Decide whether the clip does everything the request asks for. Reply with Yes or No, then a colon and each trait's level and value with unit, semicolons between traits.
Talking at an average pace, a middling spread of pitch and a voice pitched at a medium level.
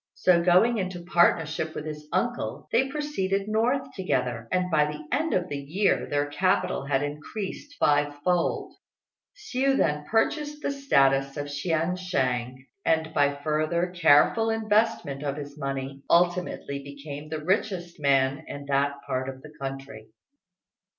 Yes: average, 145 wpm; average, 5.0 semitones; medium, 155 Hz